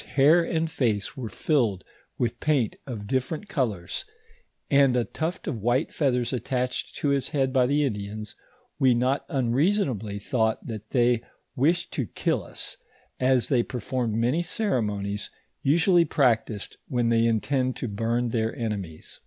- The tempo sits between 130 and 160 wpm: Yes, average, 155 wpm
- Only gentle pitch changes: No, average, 3.9 semitones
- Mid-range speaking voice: No, low, 125 Hz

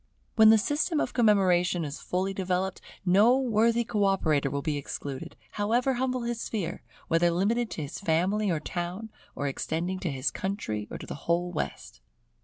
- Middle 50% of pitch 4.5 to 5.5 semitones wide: Yes, average, 5.1 semitones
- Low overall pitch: No, high, 190 Hz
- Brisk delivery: No, average, 175 wpm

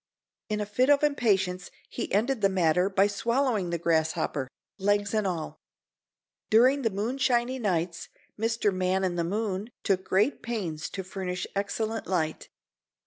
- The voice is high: Yes, high, 200 Hz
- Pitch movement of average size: Yes, average, 3.7 semitones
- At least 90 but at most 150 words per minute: Yes, average, 140 wpm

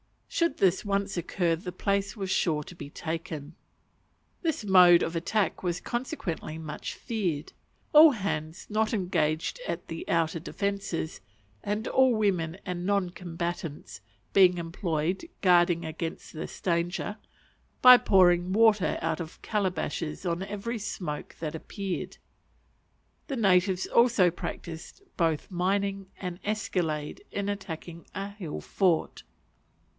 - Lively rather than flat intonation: No, average, 3.4 semitones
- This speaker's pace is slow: Yes, slow, 125 wpm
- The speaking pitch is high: No, medium, 180 Hz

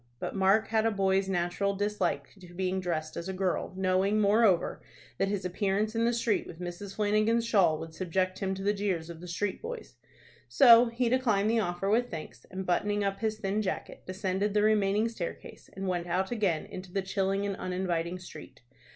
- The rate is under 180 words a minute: No, average, 195 wpm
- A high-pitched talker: Yes, high, 195 Hz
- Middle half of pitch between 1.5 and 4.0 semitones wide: Yes, narrow, 2.5 semitones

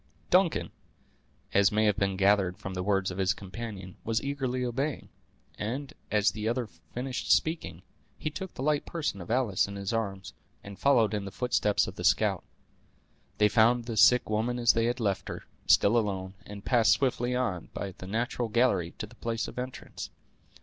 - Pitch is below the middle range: Yes, low, 110 Hz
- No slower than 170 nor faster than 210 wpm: Yes, average, 185 wpm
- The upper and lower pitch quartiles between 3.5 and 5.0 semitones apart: Yes, average, 3.9 semitones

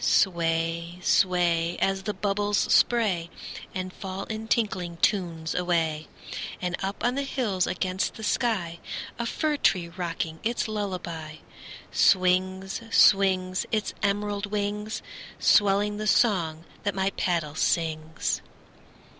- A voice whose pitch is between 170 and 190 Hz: Yes, medium, 185 Hz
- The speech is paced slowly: Yes, slow, 120 wpm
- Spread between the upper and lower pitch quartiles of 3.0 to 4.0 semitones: Yes, average, 3.4 semitones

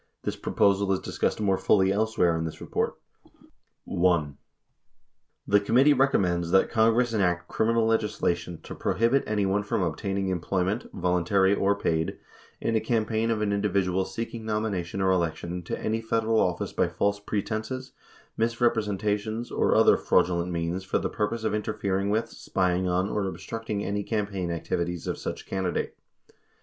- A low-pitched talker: Yes, low, 100 Hz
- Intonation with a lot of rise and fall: No, average, 3.3 semitones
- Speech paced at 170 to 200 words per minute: No, average, 160 wpm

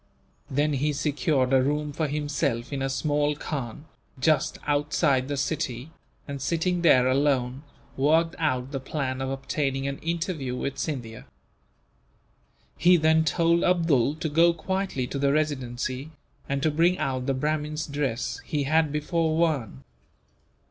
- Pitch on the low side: No, medium, 145 Hz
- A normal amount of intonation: Yes, average, 3.0 semitones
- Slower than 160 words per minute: Yes, average, 145 wpm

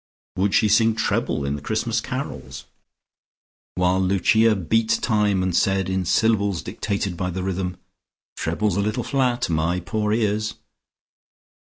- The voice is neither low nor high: No, low, 100 Hz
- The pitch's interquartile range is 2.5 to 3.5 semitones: Yes, average, 2.9 semitones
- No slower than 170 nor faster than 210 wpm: No, average, 140 wpm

